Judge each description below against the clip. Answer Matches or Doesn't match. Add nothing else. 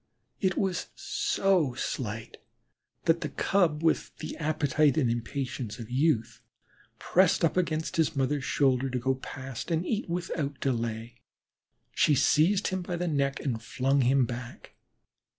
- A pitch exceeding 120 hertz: Matches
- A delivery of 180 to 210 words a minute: Doesn't match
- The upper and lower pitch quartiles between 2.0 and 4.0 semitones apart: Doesn't match